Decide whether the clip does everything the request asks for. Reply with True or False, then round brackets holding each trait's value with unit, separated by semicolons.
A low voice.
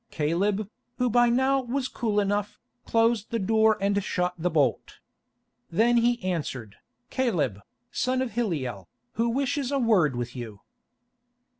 False (210 Hz)